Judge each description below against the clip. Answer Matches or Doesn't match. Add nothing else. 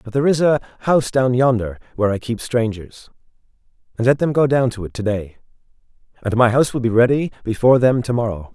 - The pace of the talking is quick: Matches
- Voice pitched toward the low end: Matches